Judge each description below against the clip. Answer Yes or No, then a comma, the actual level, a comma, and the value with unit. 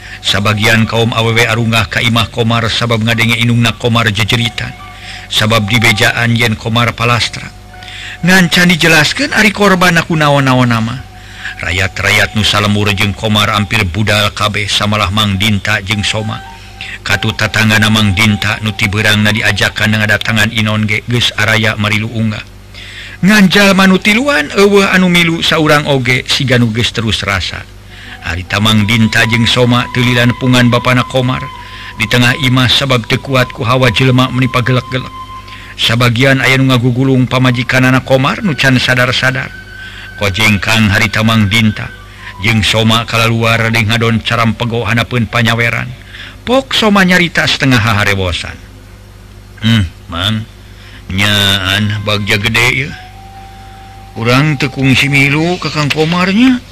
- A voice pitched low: Yes, low, 115 Hz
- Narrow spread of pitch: No, average, 3.5 semitones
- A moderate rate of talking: Yes, average, 125 wpm